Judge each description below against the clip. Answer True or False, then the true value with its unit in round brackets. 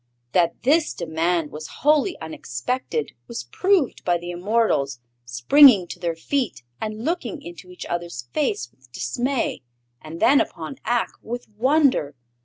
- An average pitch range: False (8.5 semitones)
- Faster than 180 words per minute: False (140 wpm)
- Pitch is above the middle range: False (180 Hz)